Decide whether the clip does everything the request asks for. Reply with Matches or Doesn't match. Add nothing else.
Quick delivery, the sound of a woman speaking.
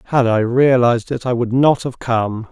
Doesn't match